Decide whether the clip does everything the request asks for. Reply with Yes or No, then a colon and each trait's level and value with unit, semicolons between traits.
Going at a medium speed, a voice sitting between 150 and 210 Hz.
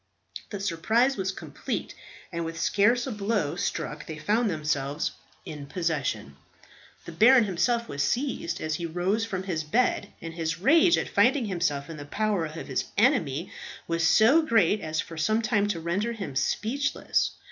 Yes: average, 170 wpm; medium, 185 Hz